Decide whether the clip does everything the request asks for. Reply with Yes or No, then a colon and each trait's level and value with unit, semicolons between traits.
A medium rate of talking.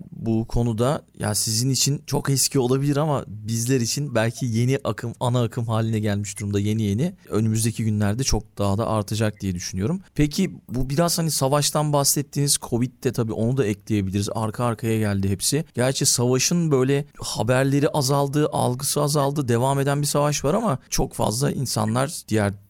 No: fast, 165 wpm